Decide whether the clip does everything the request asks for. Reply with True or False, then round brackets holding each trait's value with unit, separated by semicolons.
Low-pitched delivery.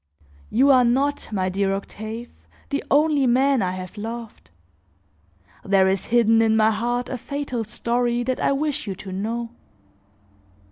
False (235 Hz)